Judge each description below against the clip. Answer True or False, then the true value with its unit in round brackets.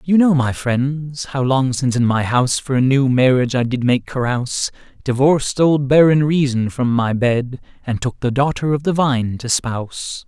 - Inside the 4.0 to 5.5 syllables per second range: True (4.9 syllables/s)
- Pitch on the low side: True (130 Hz)